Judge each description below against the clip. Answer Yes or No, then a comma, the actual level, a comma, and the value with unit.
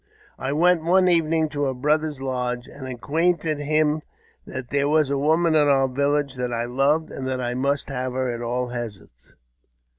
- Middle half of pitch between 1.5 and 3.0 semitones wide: No, average, 3.5 semitones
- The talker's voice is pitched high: No, medium, 140 Hz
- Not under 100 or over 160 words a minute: No, average, 185 wpm